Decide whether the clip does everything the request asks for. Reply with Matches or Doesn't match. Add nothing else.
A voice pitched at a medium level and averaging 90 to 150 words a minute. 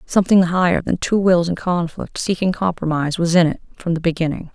Doesn't match